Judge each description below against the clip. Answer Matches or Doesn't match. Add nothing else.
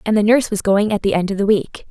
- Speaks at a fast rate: Matches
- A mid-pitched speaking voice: Doesn't match